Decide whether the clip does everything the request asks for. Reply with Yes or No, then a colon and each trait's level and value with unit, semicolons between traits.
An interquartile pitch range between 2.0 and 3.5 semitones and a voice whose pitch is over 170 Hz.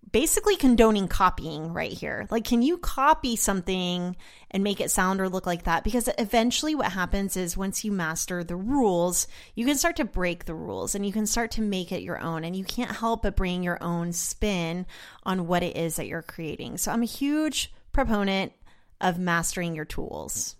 No: average, 4.6 semitones; high, 190 Hz